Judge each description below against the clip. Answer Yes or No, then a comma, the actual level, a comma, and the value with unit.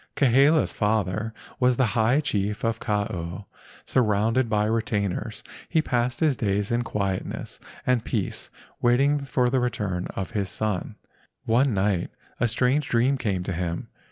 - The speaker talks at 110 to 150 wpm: Yes, average, 145 wpm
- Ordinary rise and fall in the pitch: Yes, average, 3.7 semitones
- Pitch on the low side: Yes, low, 115 Hz